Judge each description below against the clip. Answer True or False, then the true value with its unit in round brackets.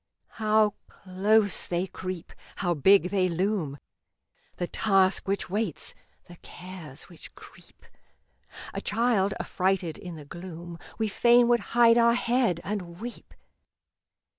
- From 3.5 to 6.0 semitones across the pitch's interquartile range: True (3.8 semitones)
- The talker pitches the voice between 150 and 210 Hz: True (190 Hz)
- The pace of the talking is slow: True (125 wpm)